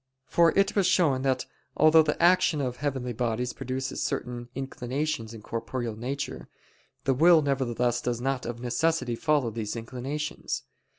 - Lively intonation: No, average, 3.9 semitones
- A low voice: Yes, low, 130 Hz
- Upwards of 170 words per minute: No, average, 145 wpm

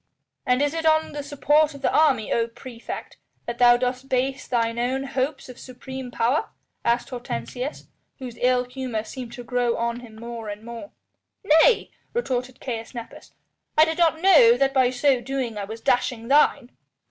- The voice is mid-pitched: No, very high, 250 Hz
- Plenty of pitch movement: No, narrow, 2.6 semitones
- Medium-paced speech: Yes, average, 175 wpm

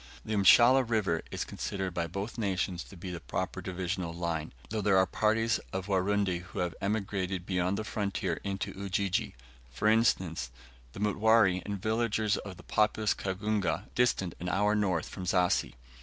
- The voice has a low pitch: Yes, very low, 95 Hz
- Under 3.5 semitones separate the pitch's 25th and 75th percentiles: Yes, average, 2.7 semitones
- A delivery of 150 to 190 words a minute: Yes, average, 160 wpm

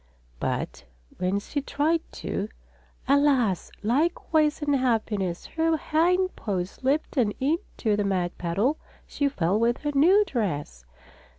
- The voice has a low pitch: No, very high, 260 Hz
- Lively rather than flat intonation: Yes, wide, 7.4 semitones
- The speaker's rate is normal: No, slow, 120 wpm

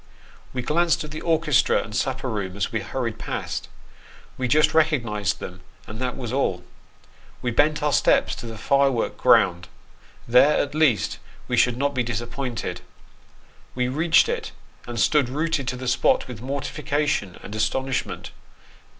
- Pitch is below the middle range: Yes, low, 130 Hz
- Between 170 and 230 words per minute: No, average, 160 wpm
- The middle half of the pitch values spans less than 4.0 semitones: No, average, 4.5 semitones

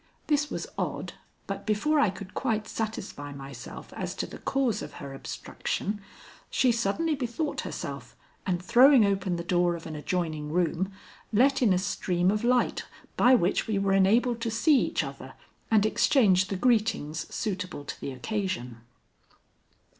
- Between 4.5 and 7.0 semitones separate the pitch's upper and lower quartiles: Yes, average, 5.1 semitones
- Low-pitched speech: No, high, 200 Hz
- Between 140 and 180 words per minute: Yes, average, 160 wpm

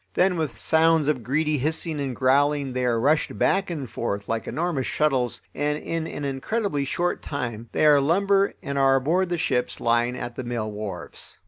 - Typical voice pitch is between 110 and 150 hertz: Yes, medium, 140 Hz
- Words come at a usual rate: Yes, average, 190 wpm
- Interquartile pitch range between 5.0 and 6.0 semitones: No, average, 4.5 semitones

